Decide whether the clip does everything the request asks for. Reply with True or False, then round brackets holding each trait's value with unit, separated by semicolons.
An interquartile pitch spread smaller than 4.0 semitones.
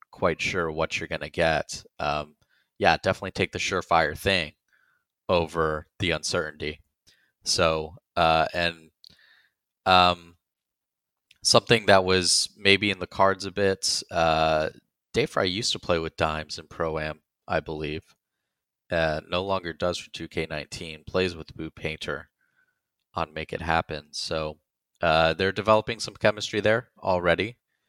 True (3.5 semitones)